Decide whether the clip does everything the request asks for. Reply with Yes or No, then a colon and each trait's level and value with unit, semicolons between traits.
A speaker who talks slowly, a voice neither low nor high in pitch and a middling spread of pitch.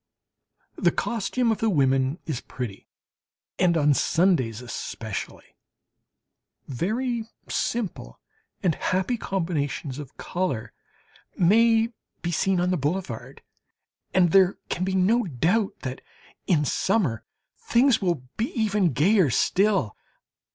No: slow, 115 wpm; medium, 180 Hz; wide, 6.9 semitones